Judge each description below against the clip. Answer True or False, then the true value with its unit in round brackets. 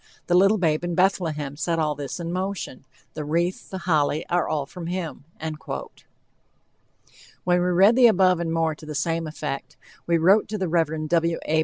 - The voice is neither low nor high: True (170 Hz)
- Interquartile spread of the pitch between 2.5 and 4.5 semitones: True (2.8 semitones)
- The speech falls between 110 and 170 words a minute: False (185 wpm)